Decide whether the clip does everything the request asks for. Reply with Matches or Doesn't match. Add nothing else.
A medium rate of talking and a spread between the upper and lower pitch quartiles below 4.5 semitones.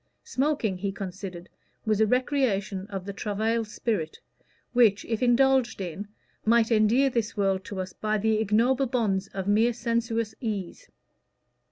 Matches